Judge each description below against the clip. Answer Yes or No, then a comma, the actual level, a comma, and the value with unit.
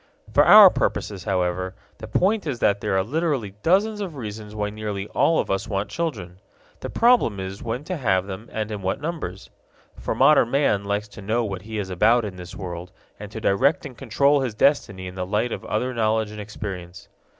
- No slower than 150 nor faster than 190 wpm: No, fast, 205 wpm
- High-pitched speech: No, low, 105 Hz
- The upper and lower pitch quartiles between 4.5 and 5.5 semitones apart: Yes, average, 5.1 semitones